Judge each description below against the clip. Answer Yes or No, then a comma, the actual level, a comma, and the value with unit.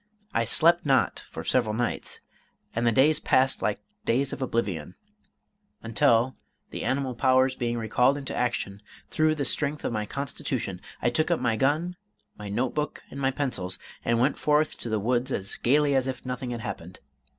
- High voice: No, low, 125 Hz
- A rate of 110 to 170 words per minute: No, average, 180 wpm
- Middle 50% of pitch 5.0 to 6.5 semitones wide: No, average, 3.4 semitones